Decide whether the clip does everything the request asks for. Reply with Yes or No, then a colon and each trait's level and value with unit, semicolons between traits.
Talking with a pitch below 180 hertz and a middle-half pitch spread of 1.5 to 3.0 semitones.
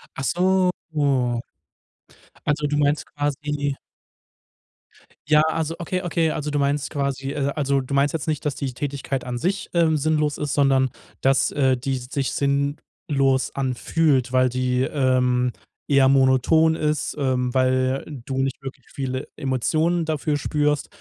Yes: medium, 140 Hz; narrow, 2.4 semitones